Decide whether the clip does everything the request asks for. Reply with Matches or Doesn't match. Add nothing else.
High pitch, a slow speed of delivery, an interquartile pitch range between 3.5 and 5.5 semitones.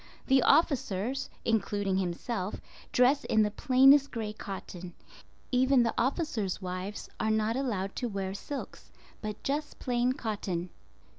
Matches